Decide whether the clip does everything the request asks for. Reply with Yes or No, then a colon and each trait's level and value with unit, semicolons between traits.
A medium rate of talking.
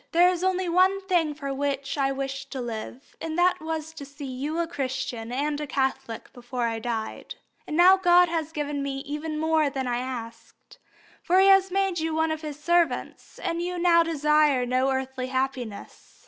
Yes: average, 190 wpm